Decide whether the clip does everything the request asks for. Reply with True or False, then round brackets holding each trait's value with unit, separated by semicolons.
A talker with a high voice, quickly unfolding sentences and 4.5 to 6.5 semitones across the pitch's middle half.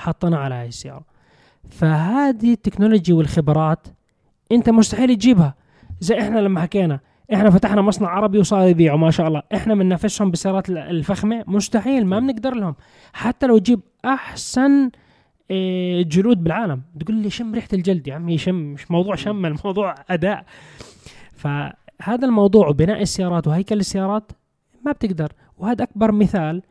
True (195 Hz; 140 wpm; 4.8 semitones)